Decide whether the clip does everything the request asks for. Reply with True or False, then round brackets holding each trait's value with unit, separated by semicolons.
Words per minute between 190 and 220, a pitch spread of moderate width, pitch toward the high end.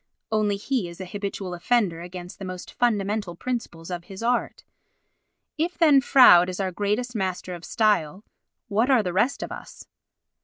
False (165 wpm; 4.7 semitones; 200 Hz)